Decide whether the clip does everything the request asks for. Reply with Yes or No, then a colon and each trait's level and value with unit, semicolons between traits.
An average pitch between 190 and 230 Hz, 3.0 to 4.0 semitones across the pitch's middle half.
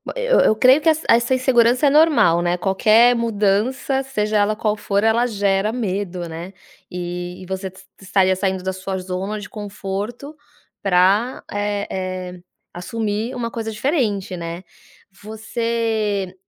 Yes: high, 210 Hz; average, 3.6 semitones